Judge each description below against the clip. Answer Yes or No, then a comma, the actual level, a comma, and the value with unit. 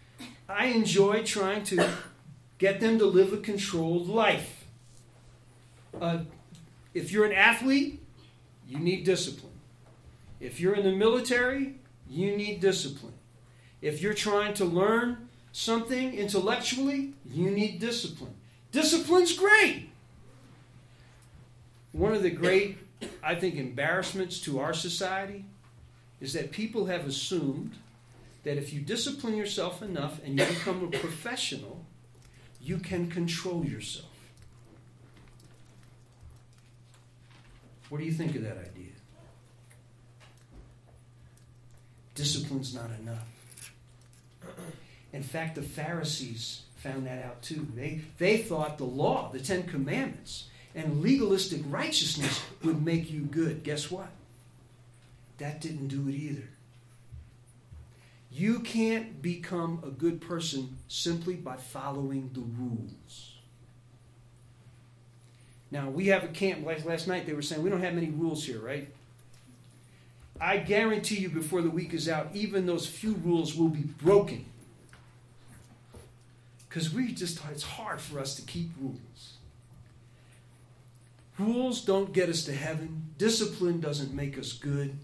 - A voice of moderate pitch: Yes, medium, 145 Hz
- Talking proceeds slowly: Yes, slow, 125 wpm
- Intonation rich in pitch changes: Yes, wide, 7.0 semitones